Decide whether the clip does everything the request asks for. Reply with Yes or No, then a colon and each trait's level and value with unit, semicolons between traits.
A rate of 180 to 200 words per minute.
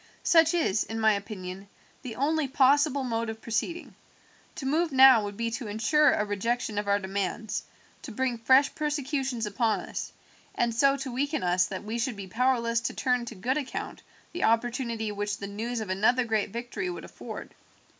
Yes: average, 185 wpm